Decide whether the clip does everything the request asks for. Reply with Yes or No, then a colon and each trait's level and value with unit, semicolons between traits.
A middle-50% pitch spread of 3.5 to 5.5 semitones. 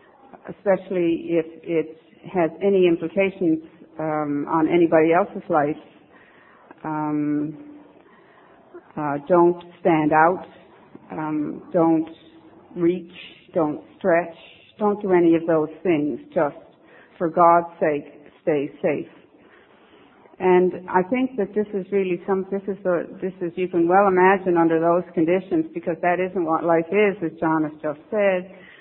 No: average, 2.8 semitones